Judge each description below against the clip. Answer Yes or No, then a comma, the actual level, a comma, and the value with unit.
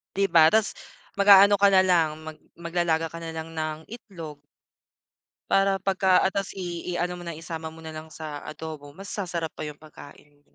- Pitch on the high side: No, medium, 165 Hz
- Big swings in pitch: No, average, 3.2 semitones